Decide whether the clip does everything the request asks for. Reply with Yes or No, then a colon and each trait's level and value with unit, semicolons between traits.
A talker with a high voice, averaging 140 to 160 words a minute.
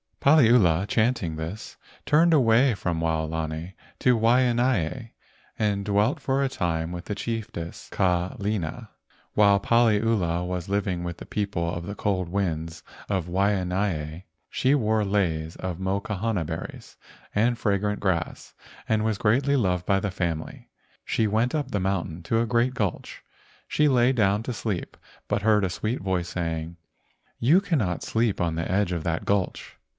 No: low, 100 Hz; average, 155 wpm